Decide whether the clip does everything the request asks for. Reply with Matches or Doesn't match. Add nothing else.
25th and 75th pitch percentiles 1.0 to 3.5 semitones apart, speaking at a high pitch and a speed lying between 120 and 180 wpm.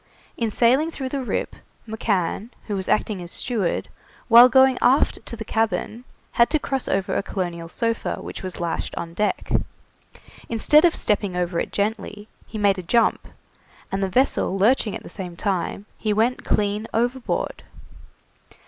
Doesn't match